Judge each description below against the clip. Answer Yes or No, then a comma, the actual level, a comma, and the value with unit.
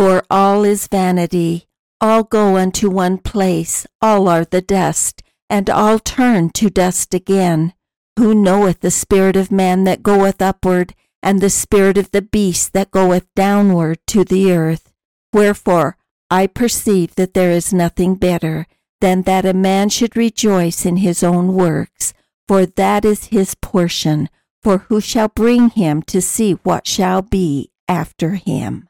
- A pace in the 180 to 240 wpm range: No, average, 155 wpm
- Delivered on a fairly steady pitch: Yes, narrow, 2.1 semitones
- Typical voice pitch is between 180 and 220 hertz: Yes, high, 190 Hz